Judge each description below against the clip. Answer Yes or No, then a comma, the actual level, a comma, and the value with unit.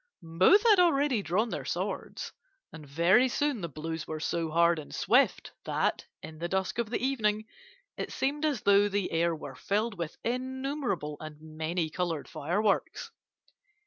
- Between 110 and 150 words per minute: No, average, 160 wpm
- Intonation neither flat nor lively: No, wide, 7.2 semitones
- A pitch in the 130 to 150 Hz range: No, high, 190 Hz